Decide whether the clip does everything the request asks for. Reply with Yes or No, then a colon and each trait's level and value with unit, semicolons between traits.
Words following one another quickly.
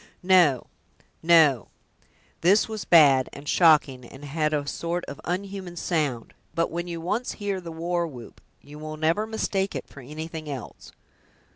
No: average, 155 wpm